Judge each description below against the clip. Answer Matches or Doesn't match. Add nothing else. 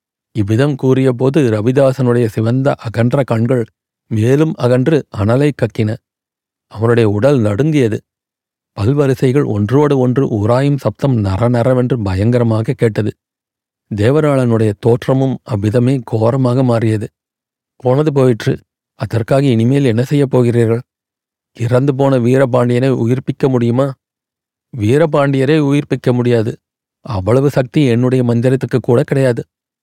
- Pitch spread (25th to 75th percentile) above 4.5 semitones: Doesn't match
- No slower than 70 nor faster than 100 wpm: Matches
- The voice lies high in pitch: Doesn't match